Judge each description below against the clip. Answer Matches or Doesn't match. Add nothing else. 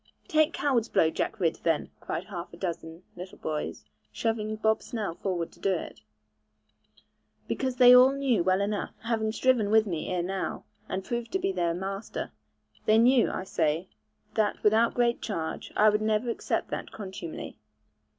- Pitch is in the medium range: Doesn't match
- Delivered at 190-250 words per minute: Doesn't match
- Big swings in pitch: Doesn't match